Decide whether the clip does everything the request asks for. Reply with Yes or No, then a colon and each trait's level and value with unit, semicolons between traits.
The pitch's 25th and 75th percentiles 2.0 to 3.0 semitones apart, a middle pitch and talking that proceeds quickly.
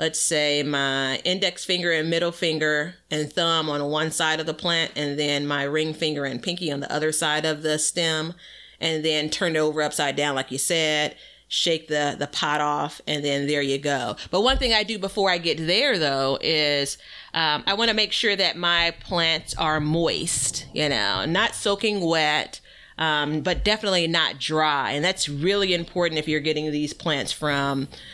No: narrow, 2.6 semitones; medium, 155 Hz; average, 195 wpm